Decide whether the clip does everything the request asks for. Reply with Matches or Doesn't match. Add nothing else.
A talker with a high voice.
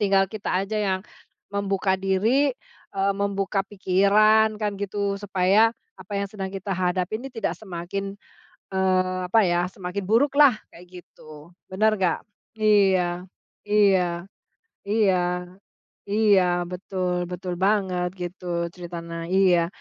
Matches